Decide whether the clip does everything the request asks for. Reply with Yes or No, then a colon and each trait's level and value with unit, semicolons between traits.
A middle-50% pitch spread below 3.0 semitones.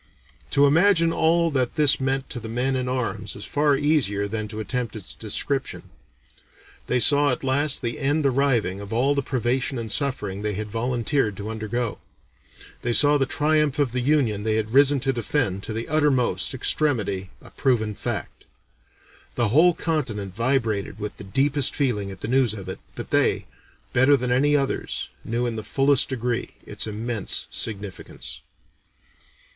No: average, 4.6 semitones